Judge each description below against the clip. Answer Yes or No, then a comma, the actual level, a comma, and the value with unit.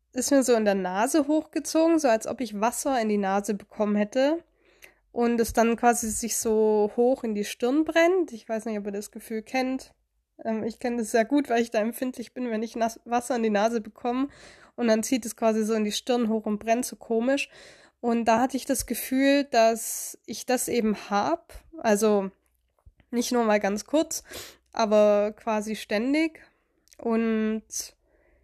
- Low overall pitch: No, high, 230 Hz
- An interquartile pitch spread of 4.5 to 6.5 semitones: No, average, 3.1 semitones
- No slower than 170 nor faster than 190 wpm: Yes, average, 185 wpm